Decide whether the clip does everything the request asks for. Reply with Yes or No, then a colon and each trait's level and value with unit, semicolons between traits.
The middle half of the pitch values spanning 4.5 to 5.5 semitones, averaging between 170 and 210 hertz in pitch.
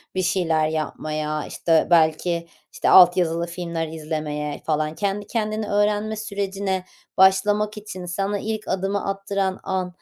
No: average, 3.8 semitones; medium, 185 Hz